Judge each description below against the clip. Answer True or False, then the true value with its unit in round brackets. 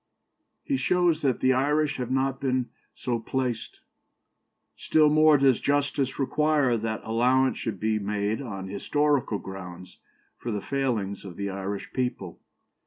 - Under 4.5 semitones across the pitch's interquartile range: False (5.3 semitones)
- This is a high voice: False (125 Hz)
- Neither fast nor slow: True (145 wpm)